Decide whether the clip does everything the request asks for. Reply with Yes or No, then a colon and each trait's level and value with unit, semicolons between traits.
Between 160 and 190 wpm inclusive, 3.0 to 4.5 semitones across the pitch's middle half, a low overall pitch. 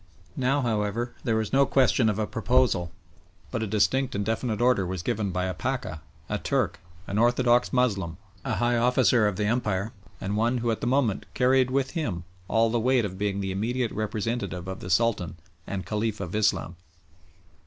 Yes: average, 185 wpm; average, 3.7 semitones; low, 110 Hz